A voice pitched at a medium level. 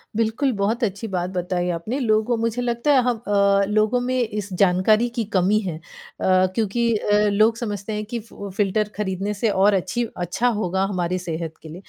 No: high, 210 Hz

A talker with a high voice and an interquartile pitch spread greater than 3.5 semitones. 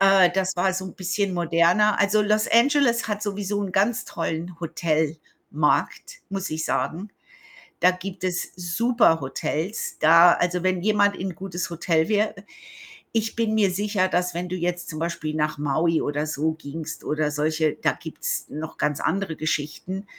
No: medium, 180 Hz; average, 4.0 semitones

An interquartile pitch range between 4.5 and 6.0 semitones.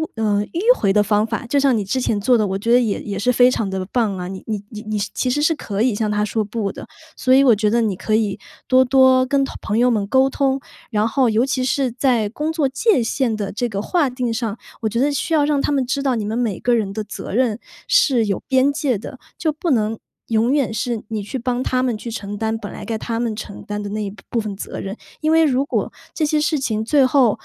No: average, 3.9 semitones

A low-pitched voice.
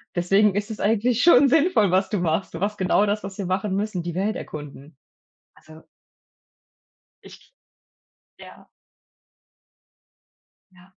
No: high, 200 Hz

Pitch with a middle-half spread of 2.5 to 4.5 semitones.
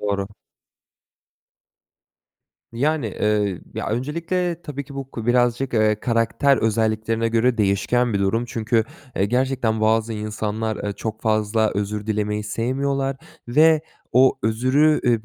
Yes: average, 3.4 semitones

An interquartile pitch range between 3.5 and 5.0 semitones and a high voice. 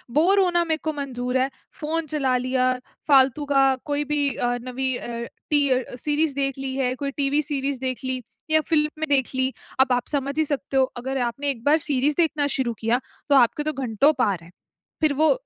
No: narrow, 2.5 semitones; very high, 275 Hz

